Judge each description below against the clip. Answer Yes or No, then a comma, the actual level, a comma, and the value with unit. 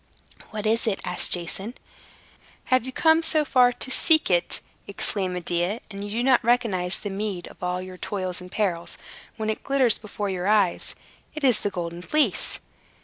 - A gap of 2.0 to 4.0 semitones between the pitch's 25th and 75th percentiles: No, average, 5.1 semitones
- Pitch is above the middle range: Yes, high, 205 Hz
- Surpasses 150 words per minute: Yes, average, 180 wpm